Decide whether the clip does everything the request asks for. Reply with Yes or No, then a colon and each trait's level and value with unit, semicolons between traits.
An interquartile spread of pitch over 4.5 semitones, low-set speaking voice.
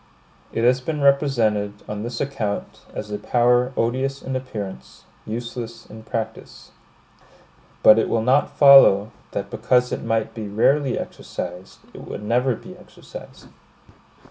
No: average, 3.5 semitones; low, 115 Hz